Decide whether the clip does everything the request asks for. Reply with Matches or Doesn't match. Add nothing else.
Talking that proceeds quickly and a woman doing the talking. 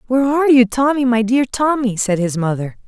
Matches